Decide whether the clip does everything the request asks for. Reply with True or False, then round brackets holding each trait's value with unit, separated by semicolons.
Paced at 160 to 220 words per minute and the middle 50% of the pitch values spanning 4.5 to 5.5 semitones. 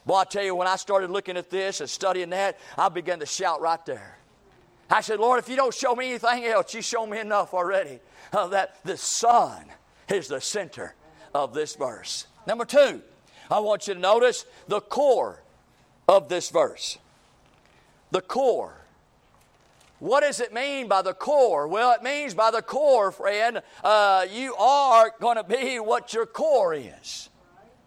True (175 wpm; 4.9 semitones)